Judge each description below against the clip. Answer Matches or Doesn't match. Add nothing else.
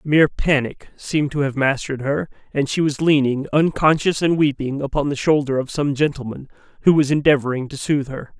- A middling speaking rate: Matches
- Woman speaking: Doesn't match